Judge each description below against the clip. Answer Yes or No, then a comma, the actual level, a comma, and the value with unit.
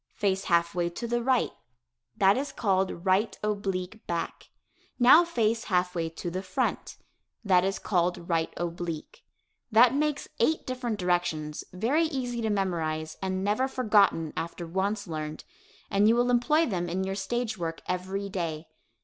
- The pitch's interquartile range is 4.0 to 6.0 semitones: Yes, average, 5.1 semitones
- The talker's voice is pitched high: Yes, high, 195 Hz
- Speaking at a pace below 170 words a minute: Yes, average, 160 wpm